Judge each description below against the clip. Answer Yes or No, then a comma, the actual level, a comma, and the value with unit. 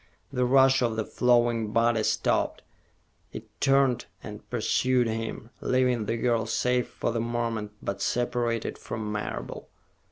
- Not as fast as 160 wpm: Yes, slow, 135 wpm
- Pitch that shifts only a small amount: Yes, narrow, 1.9 semitones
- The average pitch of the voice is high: No, low, 120 Hz